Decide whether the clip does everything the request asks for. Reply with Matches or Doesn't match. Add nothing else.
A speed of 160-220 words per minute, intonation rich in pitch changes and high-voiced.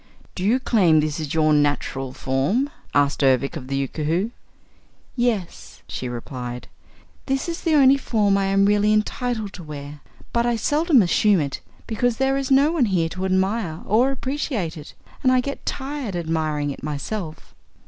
Matches